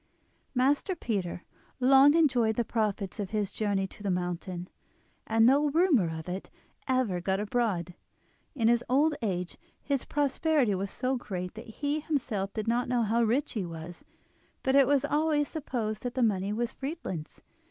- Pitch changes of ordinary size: No, wide, 5.9 semitones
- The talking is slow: No, average, 165 wpm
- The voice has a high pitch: Yes, high, 230 Hz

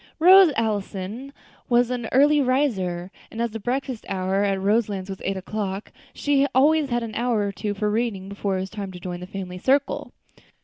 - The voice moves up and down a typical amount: Yes, average, 4.7 semitones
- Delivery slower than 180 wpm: No, average, 190 wpm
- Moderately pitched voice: No, high, 215 Hz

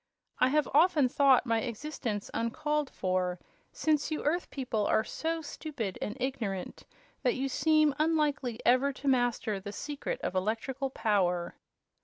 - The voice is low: No, very high, 260 Hz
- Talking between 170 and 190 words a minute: No, average, 145 wpm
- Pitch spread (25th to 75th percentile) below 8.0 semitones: Yes, wide, 5.4 semitones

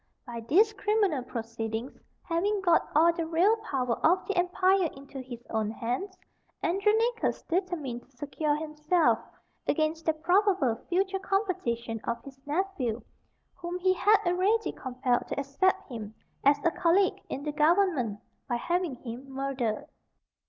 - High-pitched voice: Yes, very high, 315 Hz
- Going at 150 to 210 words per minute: No, average, 140 wpm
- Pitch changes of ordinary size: No, wide, 6.8 semitones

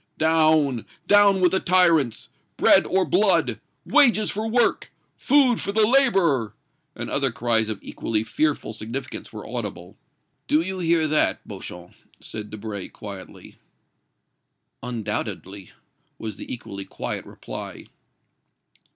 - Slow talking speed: Yes, slow, 120 wpm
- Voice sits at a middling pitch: Yes, medium, 155 Hz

